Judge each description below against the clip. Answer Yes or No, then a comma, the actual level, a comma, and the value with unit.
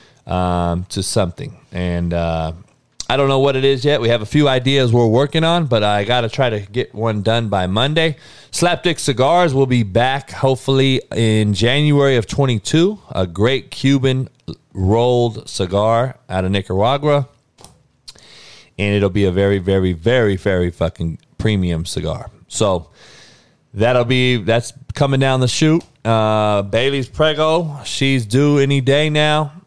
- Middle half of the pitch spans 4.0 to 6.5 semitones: Yes, average, 5.3 semitones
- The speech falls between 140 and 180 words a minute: Yes, average, 150 wpm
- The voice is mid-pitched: No, low, 120 Hz